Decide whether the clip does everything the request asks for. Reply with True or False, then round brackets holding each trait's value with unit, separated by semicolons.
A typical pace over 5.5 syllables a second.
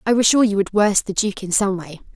True (5.8 syllables/s)